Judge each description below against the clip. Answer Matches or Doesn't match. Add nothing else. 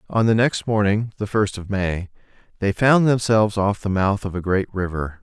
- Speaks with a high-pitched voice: Doesn't match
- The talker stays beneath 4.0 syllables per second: Doesn't match